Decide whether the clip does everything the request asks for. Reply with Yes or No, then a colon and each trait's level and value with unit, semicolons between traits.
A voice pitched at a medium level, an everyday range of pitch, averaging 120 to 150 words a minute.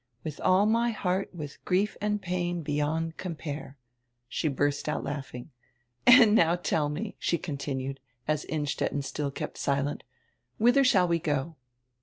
Yes: medium, 160 Hz; average, 4.2 semitones; average, 145 wpm